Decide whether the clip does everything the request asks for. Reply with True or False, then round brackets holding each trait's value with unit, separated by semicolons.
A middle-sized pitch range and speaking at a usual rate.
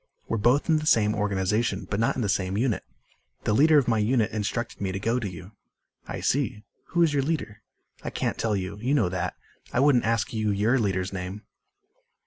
False (3.9 semitones; 210 wpm)